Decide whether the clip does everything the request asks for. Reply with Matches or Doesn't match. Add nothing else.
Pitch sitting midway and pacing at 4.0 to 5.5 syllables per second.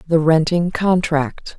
Doesn't match